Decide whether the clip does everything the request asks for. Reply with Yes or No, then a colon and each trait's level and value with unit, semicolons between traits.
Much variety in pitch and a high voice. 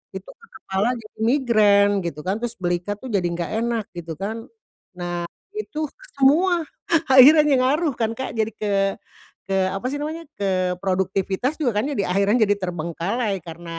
Yes: wide, 5.9 semitones; high, 205 Hz